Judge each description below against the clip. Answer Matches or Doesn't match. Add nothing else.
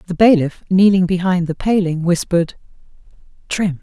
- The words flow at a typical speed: Doesn't match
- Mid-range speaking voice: Matches